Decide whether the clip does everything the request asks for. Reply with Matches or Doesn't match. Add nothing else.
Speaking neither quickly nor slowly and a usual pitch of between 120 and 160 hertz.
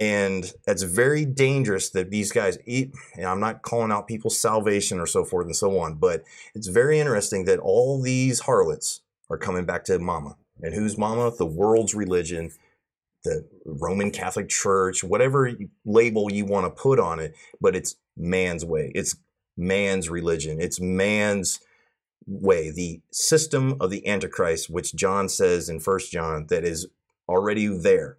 Doesn't match